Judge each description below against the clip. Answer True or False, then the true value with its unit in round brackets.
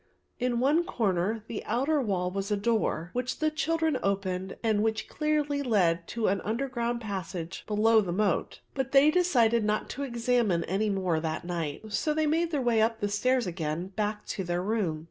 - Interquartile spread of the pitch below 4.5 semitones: False (5.1 semitones)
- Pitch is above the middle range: True (220 Hz)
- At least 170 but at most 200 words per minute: True (190 wpm)